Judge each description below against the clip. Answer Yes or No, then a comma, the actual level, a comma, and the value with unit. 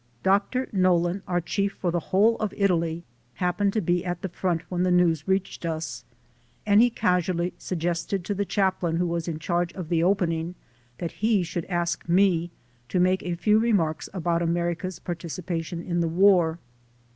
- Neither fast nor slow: Yes, average, 180 wpm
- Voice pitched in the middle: Yes, medium, 175 Hz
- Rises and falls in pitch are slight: Yes, narrow, 2.2 semitones